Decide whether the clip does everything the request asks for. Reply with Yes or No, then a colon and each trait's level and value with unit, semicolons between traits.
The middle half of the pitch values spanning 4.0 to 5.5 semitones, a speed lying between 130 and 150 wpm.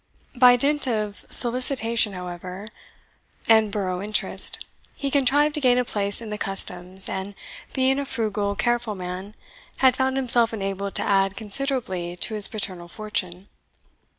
Yes: average, 4.3 semitones; average, 145 wpm